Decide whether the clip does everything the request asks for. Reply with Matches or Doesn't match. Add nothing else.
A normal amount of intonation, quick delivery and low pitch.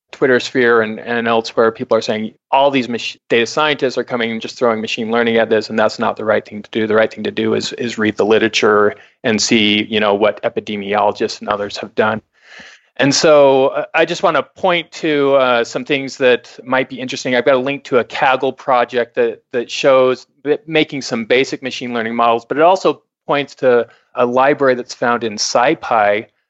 Matches